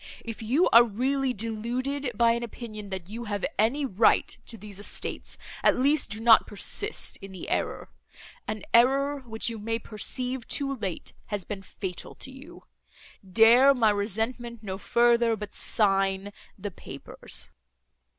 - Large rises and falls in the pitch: No, average, 3.5 semitones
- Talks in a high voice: Yes, high, 230 Hz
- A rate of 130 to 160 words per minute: Yes, average, 150 wpm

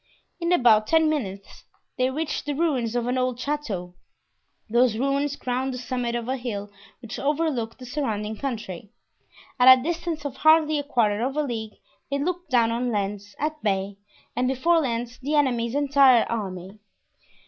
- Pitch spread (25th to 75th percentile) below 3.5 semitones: No, average, 4.3 semitones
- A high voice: Yes, very high, 250 Hz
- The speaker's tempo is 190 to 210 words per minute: No, average, 170 wpm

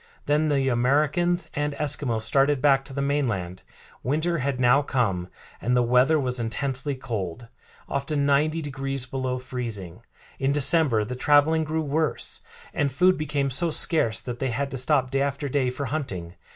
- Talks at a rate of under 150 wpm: No, average, 165 wpm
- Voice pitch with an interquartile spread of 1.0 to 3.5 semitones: Yes, average, 2.9 semitones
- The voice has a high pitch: No, low, 135 Hz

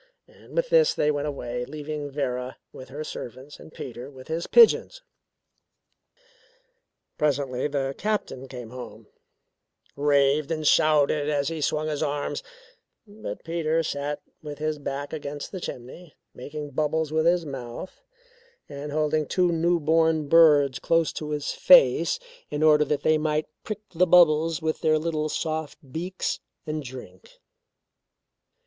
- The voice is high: No, medium, 150 Hz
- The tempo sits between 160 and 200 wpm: No, average, 140 wpm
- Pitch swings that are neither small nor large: No, narrow, 2.3 semitones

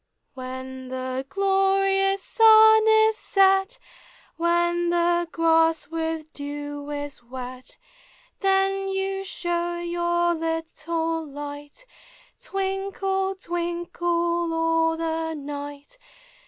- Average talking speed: No, slow, 85 wpm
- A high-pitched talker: Yes, very high, 340 Hz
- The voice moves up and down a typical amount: Yes, average, 4.4 semitones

